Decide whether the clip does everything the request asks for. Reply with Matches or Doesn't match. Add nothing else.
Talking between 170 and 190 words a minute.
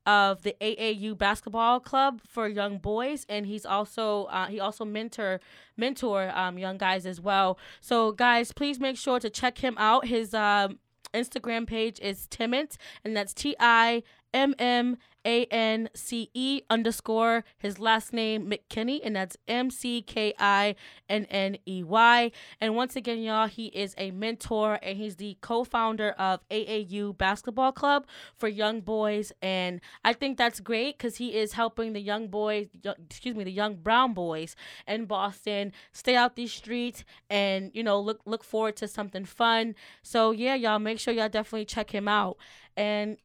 Matches